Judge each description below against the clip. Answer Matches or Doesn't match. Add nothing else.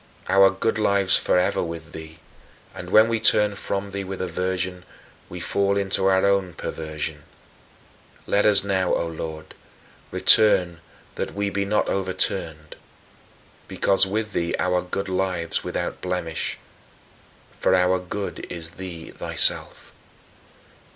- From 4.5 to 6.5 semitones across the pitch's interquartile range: Doesn't match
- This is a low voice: Matches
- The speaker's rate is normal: Doesn't match